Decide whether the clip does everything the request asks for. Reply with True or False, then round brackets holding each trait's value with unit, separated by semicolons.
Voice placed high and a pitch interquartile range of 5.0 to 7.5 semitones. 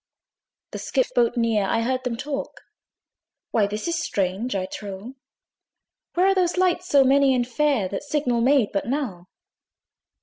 True (250 Hz; 5.5 semitones)